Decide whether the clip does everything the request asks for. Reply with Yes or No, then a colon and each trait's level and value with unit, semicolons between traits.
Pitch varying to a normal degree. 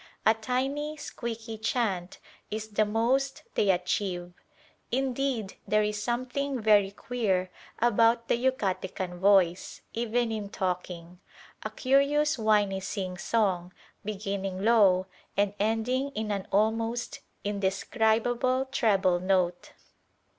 Yes: average, 3.9 semitones